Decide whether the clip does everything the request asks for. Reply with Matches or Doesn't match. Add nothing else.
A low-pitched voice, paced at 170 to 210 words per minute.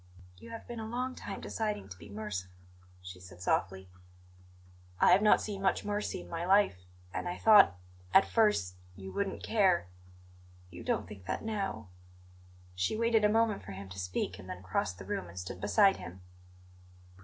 Matches